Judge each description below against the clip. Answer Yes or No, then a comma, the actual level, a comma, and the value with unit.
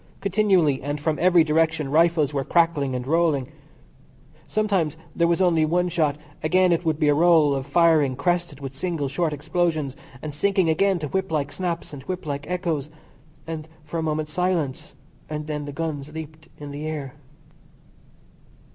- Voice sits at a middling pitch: Yes, medium, 155 Hz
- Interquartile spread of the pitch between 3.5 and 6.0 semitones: No, average, 3.0 semitones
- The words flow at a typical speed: Yes, average, 175 wpm